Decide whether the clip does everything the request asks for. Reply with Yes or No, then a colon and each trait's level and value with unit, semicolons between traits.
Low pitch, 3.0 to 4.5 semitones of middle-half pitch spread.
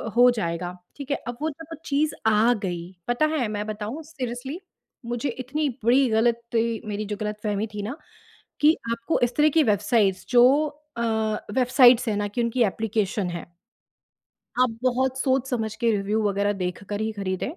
No: high, 230 Hz; average, 3.8 semitones